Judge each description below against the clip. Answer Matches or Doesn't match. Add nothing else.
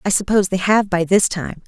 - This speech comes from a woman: Matches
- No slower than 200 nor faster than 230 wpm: Doesn't match